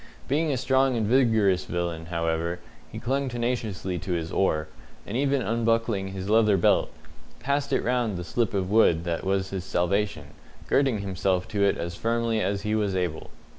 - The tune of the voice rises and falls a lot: No, average, 4.6 semitones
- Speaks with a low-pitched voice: Yes, low, 100 Hz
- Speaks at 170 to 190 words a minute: Yes, average, 175 wpm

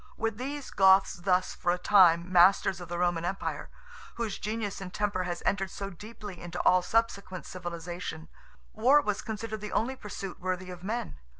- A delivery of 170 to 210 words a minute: Yes, average, 175 wpm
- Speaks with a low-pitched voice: No, high, 190 Hz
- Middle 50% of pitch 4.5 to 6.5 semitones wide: No, average, 3.0 semitones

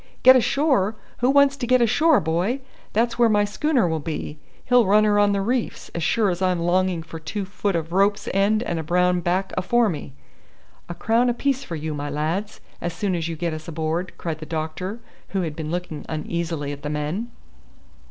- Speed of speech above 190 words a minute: Yes, fast, 205 wpm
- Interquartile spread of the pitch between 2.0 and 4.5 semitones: No, wide, 5.6 semitones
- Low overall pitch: No, medium, 185 Hz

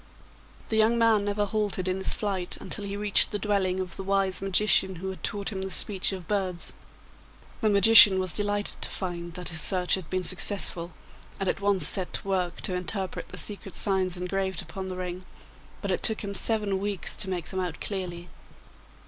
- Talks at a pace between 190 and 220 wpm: Yes, average, 200 wpm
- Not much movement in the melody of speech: Yes, narrow, 1.9 semitones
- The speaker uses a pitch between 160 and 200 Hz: Yes, high, 190 Hz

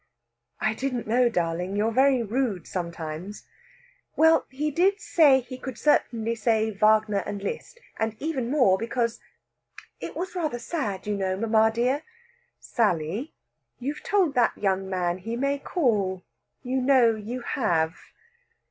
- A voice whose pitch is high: Yes, high, 230 Hz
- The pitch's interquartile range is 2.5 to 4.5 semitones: No, average, 5.0 semitones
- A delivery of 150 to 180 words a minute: No, average, 140 wpm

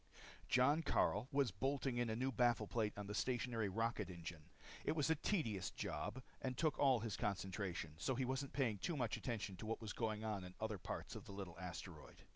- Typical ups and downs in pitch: Yes, average, 4.8 semitones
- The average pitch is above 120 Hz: No, low, 110 Hz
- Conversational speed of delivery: No, fast, 215 wpm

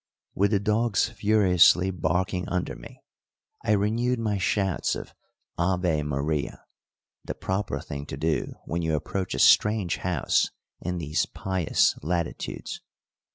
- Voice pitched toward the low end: Yes, very low, 90 Hz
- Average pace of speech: No, slow, 130 wpm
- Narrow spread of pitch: No, average, 3.9 semitones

